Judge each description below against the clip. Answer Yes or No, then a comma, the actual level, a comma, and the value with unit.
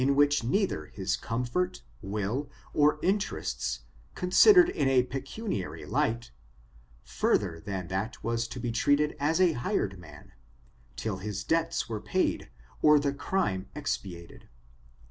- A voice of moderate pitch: No, low, 125 Hz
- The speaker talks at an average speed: No, slow, 125 wpm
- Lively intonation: Yes, wide, 7.3 semitones